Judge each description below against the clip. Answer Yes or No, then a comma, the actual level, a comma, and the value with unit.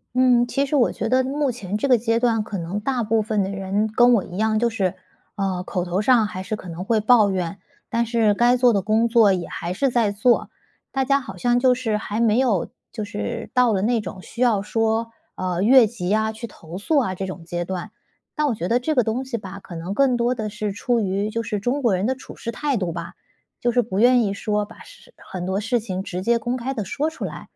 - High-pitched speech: Yes, high, 220 Hz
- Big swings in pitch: No, average, 3.8 semitones